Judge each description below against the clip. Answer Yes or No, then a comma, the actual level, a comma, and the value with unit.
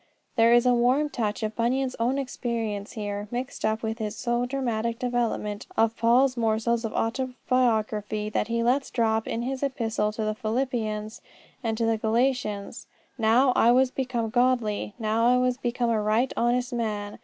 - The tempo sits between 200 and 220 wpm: No, average, 170 wpm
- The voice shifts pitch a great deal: No, narrow, 2.4 semitones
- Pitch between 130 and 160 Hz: No, high, 235 Hz